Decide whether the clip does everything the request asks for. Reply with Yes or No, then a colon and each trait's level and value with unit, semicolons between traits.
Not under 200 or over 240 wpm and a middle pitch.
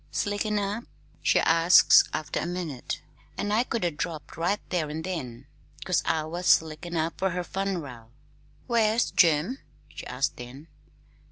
No: average, 155 wpm; medium, 170 Hz